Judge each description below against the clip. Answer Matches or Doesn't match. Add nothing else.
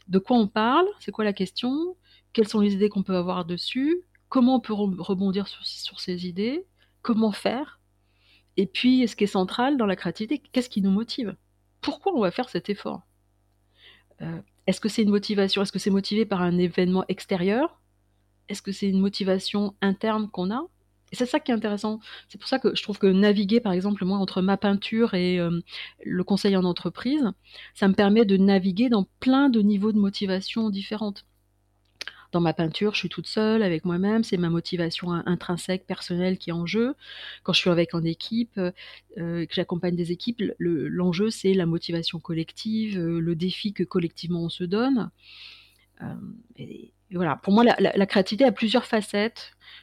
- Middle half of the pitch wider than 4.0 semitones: Doesn't match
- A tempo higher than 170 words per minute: Matches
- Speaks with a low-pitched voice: Doesn't match